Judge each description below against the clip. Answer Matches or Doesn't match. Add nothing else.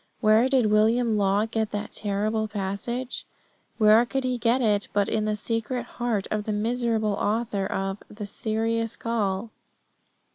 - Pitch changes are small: Matches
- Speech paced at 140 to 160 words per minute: Matches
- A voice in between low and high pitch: Doesn't match